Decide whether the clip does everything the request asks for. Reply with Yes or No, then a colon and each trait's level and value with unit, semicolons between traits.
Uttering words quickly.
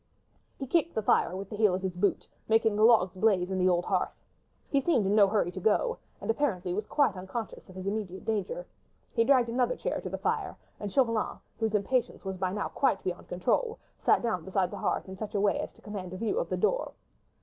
Yes: fast, 235 wpm